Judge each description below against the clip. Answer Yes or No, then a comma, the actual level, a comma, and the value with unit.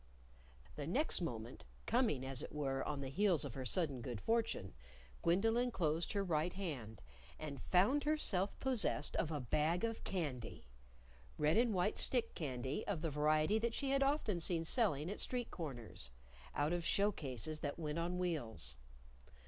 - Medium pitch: Yes, medium, 165 Hz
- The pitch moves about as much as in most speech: No, wide, 6.7 semitones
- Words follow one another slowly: No, average, 165 wpm